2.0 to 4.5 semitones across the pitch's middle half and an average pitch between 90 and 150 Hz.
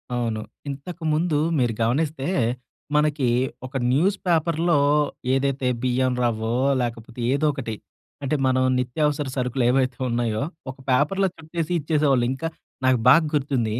Yes: average, 3.6 semitones; low, 135 Hz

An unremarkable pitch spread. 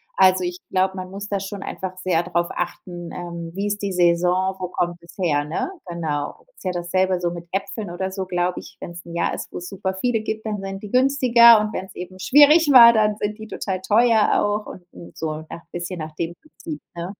Yes: average, 3.1 semitones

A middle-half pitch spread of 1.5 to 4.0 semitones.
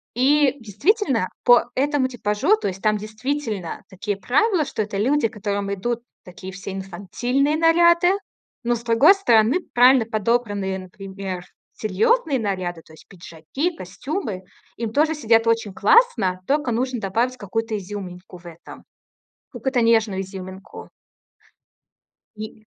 No: wide, 5.6 semitones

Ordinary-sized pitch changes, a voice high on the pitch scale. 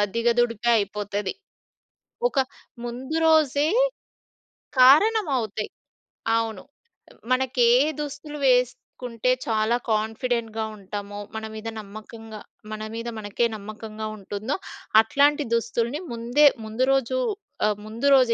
Yes: average, 3.0 semitones; high, 230 Hz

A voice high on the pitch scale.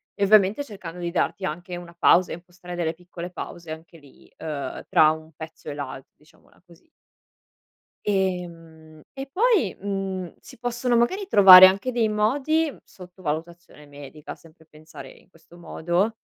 No: medium, 175 Hz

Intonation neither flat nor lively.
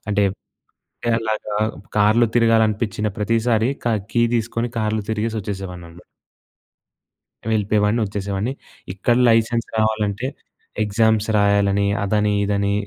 No: narrow, 1.9 semitones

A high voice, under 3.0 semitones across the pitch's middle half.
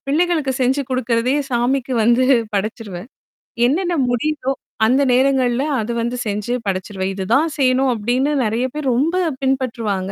No: very high, 250 Hz; average, 3.3 semitones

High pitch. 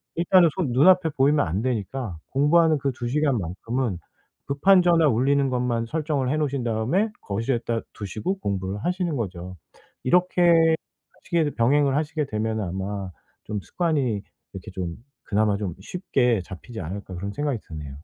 No: low, 125 Hz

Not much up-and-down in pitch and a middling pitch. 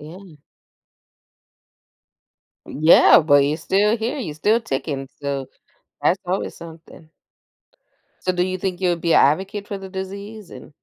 No: average, 4.2 semitones; medium, 180 Hz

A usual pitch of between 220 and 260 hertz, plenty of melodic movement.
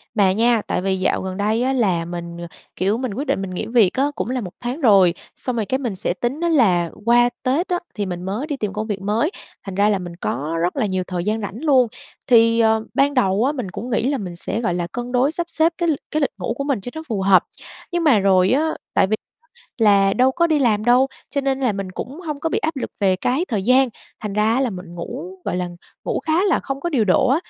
Yes: high, 225 Hz; wide, 5.8 semitones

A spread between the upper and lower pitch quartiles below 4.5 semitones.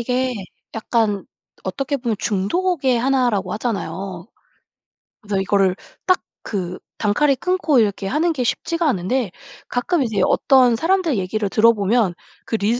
No: average, 5.2 semitones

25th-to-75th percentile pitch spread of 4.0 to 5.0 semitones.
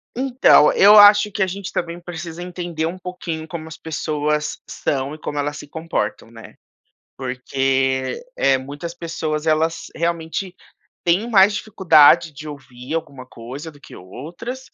No: average, 3.6 semitones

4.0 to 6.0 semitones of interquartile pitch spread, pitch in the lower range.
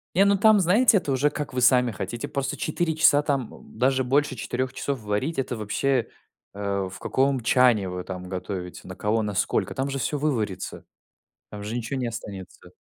Yes: average, 5.3 semitones; low, 125 Hz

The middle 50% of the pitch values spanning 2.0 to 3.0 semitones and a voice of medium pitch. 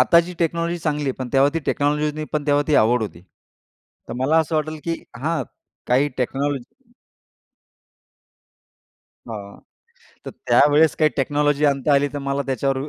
Yes: narrow, 2.5 semitones; medium, 145 Hz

